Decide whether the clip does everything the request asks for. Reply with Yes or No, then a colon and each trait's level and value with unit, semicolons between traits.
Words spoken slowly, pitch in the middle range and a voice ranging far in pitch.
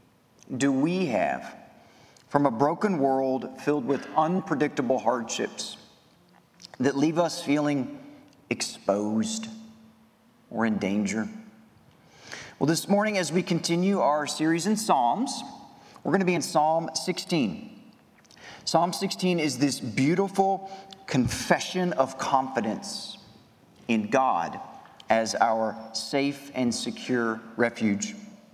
Yes: slow, 110 wpm; medium, 155 Hz; wide, 6.8 semitones